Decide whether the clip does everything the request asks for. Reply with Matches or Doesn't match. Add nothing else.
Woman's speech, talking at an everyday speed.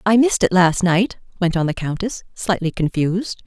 Matches